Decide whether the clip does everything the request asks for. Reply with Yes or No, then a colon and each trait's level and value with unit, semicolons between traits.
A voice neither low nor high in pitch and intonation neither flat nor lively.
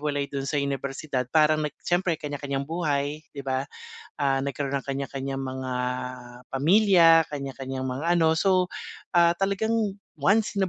Yes: medium, 145 Hz; average, 4.0 semitones